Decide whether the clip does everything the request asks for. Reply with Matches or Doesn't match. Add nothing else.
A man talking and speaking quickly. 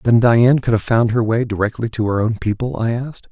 Matches